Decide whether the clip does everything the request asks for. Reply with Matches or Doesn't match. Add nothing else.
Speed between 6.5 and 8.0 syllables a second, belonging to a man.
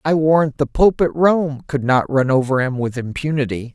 Doesn't match